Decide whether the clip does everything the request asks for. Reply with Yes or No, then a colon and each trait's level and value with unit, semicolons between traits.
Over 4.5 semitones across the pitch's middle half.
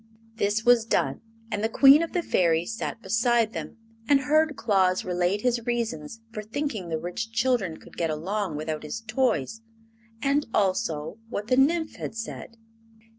Yes: average, 5.0 semitones